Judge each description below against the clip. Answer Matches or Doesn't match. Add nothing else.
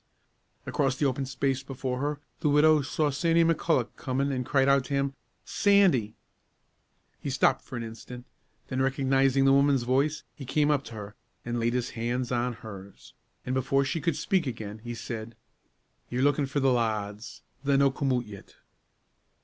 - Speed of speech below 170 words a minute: Doesn't match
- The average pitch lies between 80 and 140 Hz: Matches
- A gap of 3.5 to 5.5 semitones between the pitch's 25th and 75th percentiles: Doesn't match